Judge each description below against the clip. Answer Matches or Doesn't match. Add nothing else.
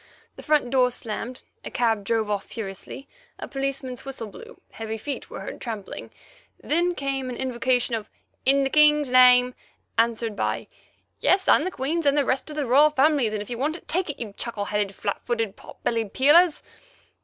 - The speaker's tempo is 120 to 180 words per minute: Doesn't match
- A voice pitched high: Matches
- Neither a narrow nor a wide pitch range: Matches